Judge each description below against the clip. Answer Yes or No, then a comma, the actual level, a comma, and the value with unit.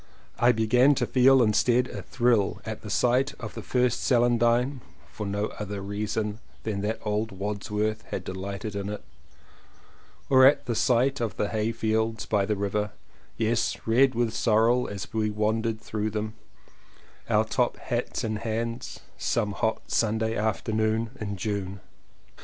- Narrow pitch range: Yes, narrow, 2.2 semitones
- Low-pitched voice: Yes, low, 110 Hz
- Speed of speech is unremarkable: Yes, average, 155 wpm